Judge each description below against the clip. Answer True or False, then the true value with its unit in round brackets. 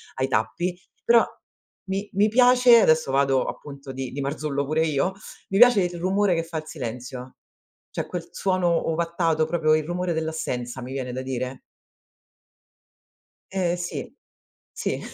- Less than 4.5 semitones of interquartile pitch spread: False (5.0 semitones)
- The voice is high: False (160 Hz)